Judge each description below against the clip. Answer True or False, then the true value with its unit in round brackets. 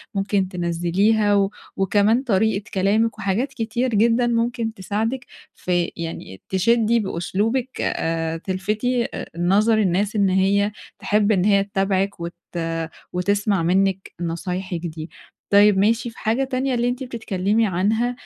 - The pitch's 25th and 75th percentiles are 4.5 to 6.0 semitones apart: False (3.3 semitones)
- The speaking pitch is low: False (205 Hz)